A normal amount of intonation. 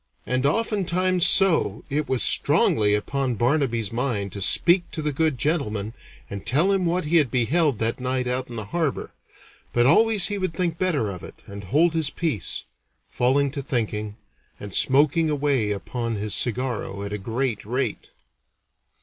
No: wide, 6.7 semitones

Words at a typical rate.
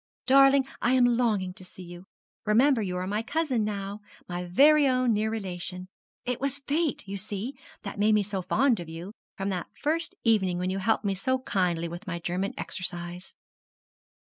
Yes: average, 185 wpm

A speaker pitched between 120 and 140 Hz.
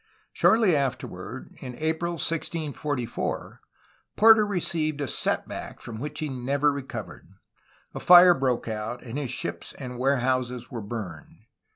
Yes: low, 135 Hz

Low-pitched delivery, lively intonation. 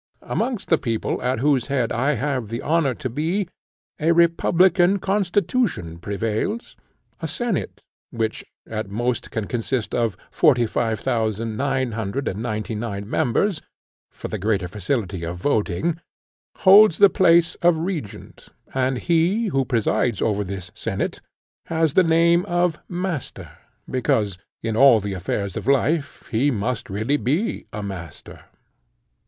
Yes: low, 130 Hz; wide, 7.5 semitones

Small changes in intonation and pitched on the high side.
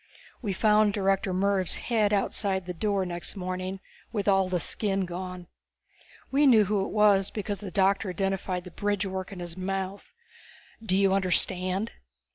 Yes: narrow, 1.8 semitones; high, 195 Hz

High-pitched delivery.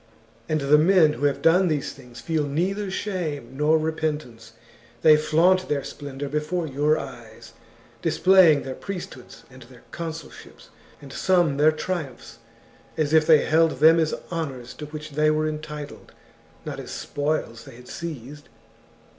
No: medium, 155 Hz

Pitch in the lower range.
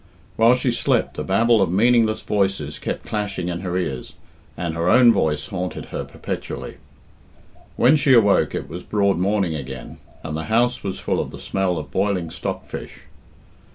Yes: very low, 95 Hz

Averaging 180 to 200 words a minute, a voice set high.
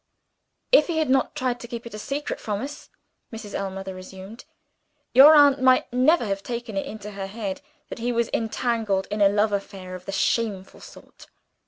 Yes: average, 185 wpm; high, 220 Hz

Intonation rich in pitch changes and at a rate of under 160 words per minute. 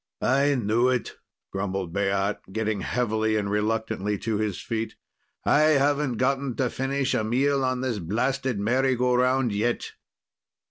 No: average, 3.8 semitones; average, 145 wpm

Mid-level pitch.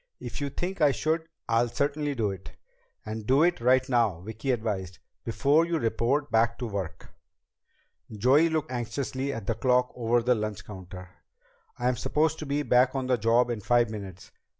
No: low, 120 Hz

